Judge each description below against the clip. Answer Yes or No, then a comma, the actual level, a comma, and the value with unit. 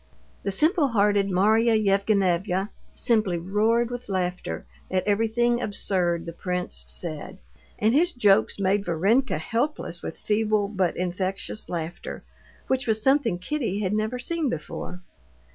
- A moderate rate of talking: No, slow, 130 wpm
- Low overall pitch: No, high, 205 Hz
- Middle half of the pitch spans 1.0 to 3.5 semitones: No, average, 3.9 semitones